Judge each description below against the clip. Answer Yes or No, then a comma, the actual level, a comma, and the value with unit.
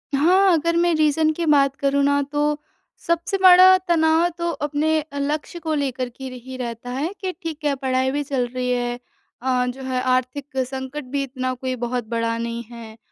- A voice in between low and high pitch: No, very high, 275 Hz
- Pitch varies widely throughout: No, average, 3.7 semitones